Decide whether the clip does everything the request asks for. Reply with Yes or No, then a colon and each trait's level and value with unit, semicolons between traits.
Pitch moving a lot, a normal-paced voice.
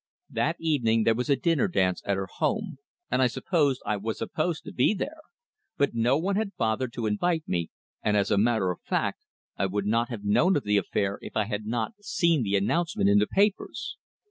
No: wide, 8.0 semitones; fast, 215 wpm